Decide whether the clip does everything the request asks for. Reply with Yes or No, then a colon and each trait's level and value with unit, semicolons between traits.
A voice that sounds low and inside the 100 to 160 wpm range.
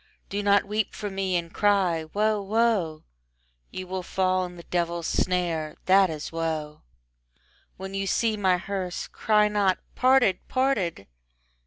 No: high, 190 Hz; average, 145 wpm